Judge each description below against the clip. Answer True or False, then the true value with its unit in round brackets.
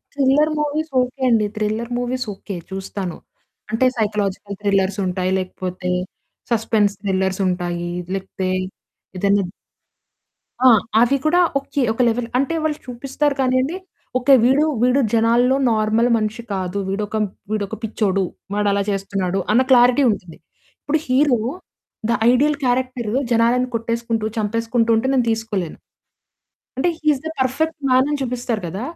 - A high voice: True (230 Hz)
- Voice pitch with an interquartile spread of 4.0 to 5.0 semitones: True (4.4 semitones)